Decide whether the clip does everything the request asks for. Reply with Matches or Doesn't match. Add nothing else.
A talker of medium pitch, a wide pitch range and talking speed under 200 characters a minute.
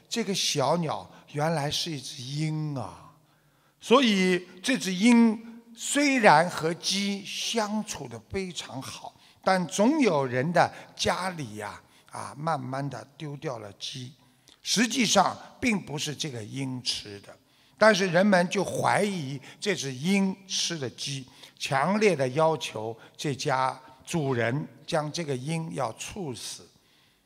Matches